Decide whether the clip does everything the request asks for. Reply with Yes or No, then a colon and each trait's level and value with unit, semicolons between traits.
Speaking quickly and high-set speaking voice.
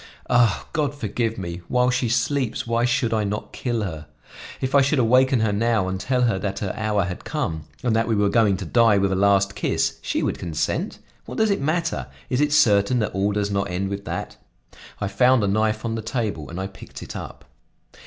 No: fast, 225 wpm; low, 110 Hz